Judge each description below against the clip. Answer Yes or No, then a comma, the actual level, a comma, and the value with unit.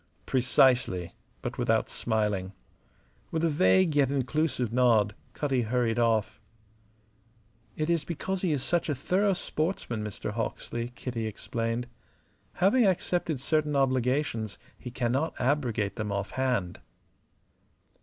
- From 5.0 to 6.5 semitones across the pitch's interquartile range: Yes, average, 5.3 semitones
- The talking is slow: Yes, slow, 120 wpm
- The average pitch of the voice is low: Yes, low, 125 Hz